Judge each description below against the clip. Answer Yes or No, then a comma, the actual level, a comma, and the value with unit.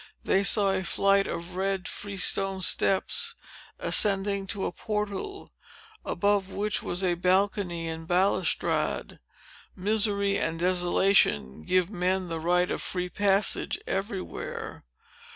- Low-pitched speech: No, high, 190 Hz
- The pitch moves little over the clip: Yes, narrow, 2.0 semitones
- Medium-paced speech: No, slow, 115 wpm